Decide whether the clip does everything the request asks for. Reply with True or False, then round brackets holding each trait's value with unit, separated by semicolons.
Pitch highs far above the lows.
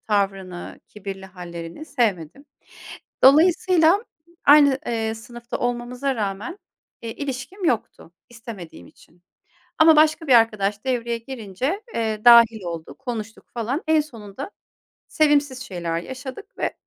True (5.7 semitones)